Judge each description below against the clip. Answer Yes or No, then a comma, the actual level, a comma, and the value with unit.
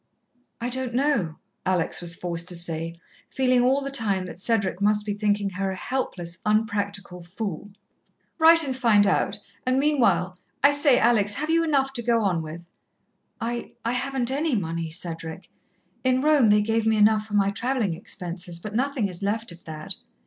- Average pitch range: No, wide, 5.9 semitones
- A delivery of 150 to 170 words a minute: No, average, 180 wpm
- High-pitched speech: Yes, high, 210 Hz